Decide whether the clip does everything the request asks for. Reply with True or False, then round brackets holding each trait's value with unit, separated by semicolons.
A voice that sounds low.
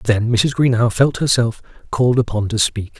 True (115 Hz)